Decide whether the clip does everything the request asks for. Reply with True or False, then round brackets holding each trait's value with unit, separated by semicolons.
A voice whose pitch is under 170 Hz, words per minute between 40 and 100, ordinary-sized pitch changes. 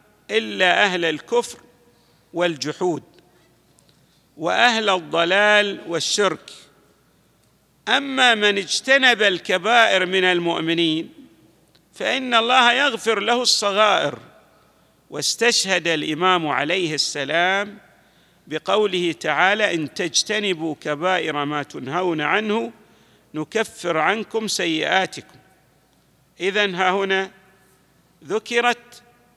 False (190 Hz; 75 wpm; 4.6 semitones)